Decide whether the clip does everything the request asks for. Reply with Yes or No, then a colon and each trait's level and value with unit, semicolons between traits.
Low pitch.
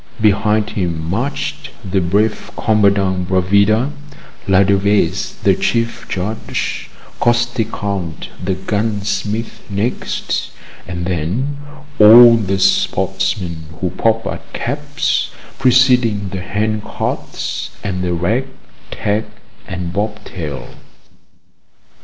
Yes: low, 100 Hz